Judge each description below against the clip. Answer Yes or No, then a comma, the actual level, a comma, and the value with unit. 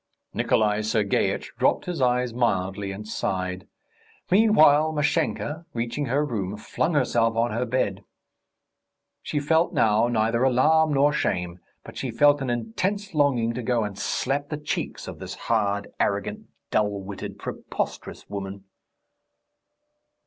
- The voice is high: No, low, 120 Hz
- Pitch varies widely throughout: Yes, wide, 5.9 semitones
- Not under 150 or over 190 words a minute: No, slow, 135 wpm